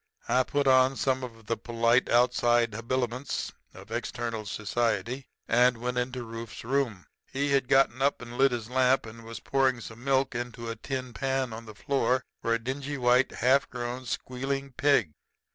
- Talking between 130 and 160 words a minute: No, average, 175 wpm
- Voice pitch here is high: No, low, 125 Hz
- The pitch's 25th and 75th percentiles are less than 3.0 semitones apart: Yes, narrow, 2.4 semitones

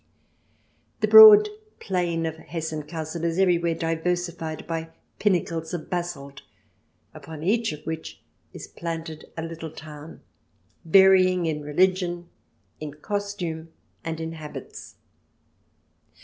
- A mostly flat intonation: Yes, narrow, 2.0 semitones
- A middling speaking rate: No, slow, 110 wpm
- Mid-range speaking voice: Yes, medium, 165 Hz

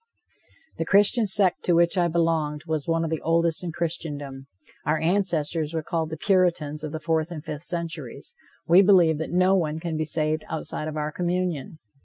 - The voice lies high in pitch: No, medium, 165 Hz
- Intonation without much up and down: Yes, narrow, 2.1 semitones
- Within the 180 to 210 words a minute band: Yes, average, 190 wpm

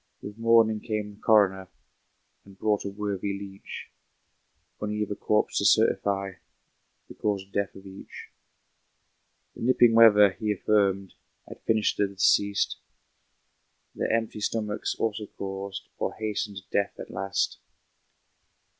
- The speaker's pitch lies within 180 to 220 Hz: No, low, 105 Hz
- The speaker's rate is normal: No, slow, 130 wpm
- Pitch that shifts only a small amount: Yes, narrow, 1.6 semitones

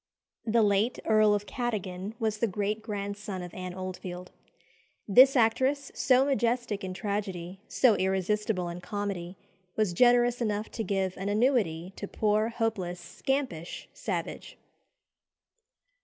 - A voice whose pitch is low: No, high, 205 Hz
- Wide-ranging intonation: No, average, 3.7 semitones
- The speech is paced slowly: Yes, slow, 125 wpm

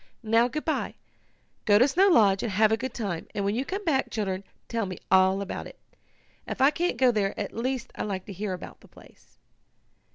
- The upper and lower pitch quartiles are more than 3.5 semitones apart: Yes, average, 4.8 semitones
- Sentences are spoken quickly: Yes, fast, 220 wpm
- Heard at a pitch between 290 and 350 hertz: No, high, 220 Hz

